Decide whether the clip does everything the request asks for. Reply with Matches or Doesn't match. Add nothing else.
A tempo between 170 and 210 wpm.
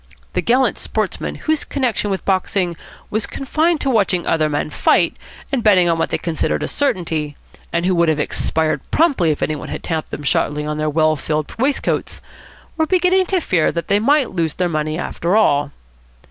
Matches